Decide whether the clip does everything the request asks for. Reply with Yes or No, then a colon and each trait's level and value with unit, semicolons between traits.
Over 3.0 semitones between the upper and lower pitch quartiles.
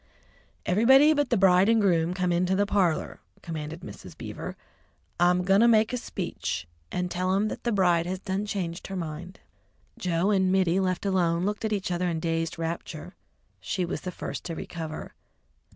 No: average, 2.7 semitones